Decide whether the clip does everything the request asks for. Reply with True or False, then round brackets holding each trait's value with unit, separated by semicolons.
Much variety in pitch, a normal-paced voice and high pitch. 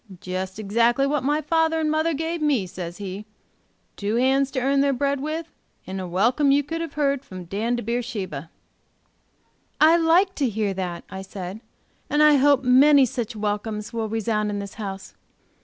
True (6.2 semitones; 180 wpm; 245 Hz)